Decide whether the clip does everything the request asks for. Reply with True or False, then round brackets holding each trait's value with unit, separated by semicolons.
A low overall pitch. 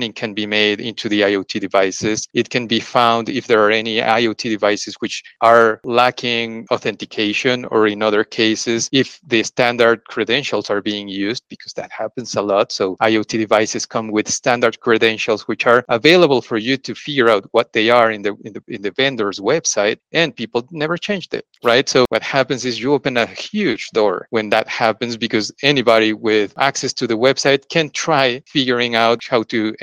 True (115 Hz)